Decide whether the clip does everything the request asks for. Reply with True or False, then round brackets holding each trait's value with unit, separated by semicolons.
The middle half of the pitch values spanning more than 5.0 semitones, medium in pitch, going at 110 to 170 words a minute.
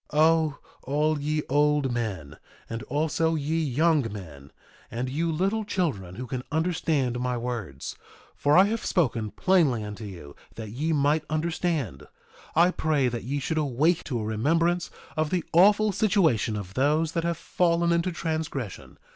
True (5.6 semitones; 150 Hz; 160 wpm)